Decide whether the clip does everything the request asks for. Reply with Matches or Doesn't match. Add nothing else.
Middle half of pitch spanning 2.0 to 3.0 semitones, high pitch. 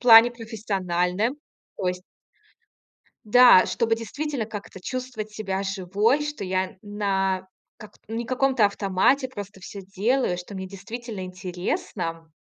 Doesn't match